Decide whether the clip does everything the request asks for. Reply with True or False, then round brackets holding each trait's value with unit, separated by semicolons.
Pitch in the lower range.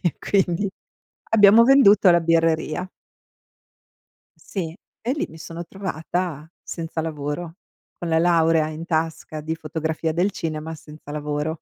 False (165 Hz)